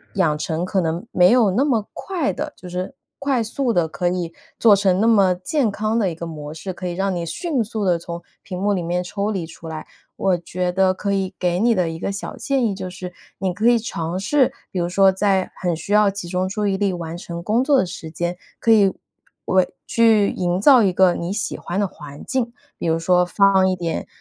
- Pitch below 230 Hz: Yes, medium, 185 Hz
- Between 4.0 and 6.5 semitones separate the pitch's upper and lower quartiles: No, average, 3.2 semitones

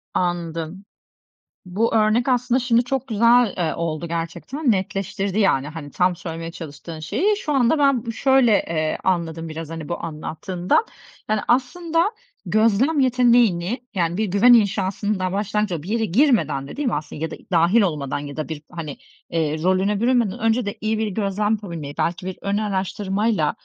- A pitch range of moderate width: No, wide, 5.8 semitones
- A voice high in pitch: Yes, high, 195 Hz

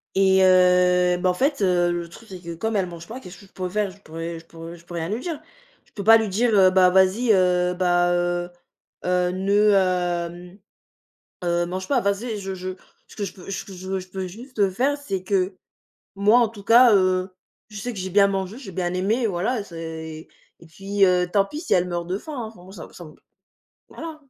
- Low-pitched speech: No, medium, 185 Hz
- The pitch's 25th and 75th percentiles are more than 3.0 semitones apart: No, narrow, 2.6 semitones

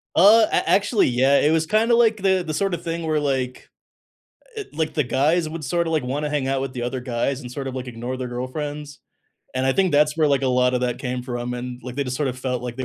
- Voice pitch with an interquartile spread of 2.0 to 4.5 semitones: Yes, average, 4.1 semitones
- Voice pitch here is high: No, medium, 140 Hz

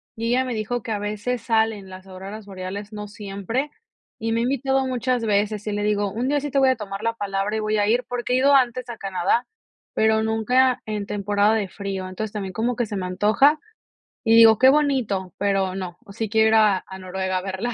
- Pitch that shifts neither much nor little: Yes, average, 3.4 semitones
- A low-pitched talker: No, high, 215 Hz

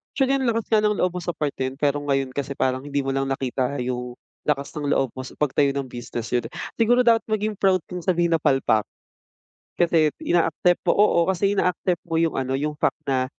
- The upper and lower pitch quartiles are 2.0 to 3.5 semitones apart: No, average, 5.3 semitones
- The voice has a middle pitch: Yes, medium, 150 Hz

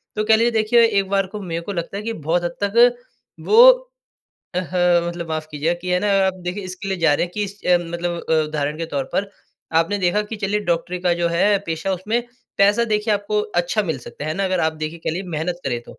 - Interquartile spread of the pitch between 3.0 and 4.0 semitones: Yes, average, 3.7 semitones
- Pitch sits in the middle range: Yes, medium, 180 Hz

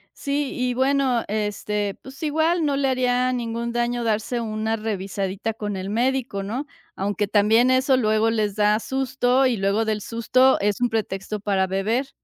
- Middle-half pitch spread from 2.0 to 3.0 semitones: No, average, 3.7 semitones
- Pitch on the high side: Yes, high, 225 Hz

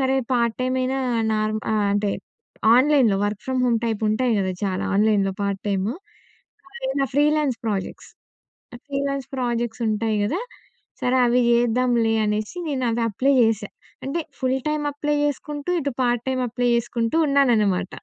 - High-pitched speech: Yes, high, 240 Hz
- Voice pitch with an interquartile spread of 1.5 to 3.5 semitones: No, average, 4.1 semitones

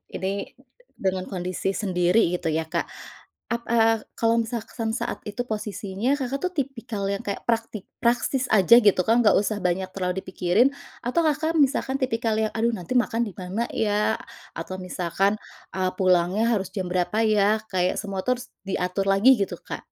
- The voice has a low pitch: No, high, 210 Hz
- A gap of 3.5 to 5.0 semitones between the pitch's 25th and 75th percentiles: Yes, average, 3.9 semitones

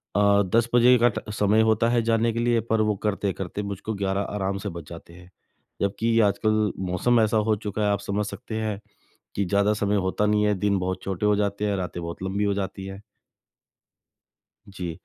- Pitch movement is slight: Yes, narrow, 1.9 semitones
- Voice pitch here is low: Yes, low, 100 Hz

